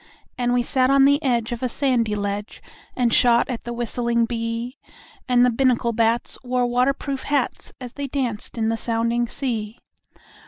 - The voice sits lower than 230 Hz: No, high, 240 Hz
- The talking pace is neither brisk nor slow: Yes, average, 180 wpm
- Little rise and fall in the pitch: Yes, narrow, 1.8 semitones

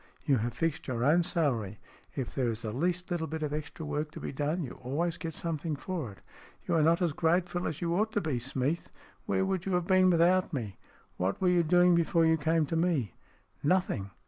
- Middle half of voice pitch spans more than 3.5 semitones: Yes, average, 4.3 semitones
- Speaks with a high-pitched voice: No, medium, 160 Hz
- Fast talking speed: Yes, fast, 225 wpm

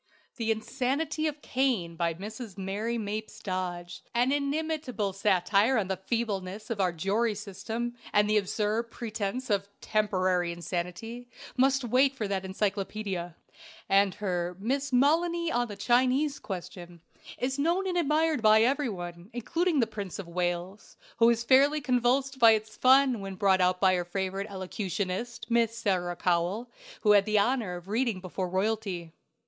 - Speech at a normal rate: Yes, average, 155 wpm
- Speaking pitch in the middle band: No, high, 215 Hz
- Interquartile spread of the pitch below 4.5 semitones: No, average, 5.0 semitones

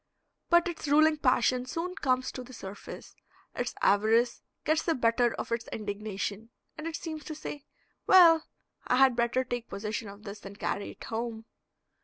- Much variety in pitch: Yes, wide, 5.9 semitones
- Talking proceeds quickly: No, average, 170 wpm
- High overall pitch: Yes, high, 245 Hz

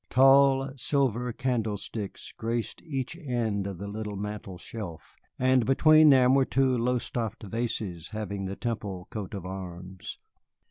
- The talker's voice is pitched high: No, low, 115 Hz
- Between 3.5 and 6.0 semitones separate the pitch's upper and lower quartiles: Yes, average, 4.6 semitones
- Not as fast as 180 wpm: Yes, slow, 135 wpm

